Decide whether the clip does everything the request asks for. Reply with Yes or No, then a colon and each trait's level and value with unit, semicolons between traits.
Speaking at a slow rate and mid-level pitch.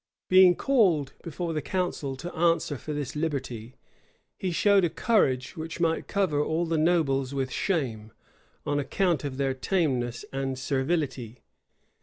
No: average, 145 wpm; medium, 150 Hz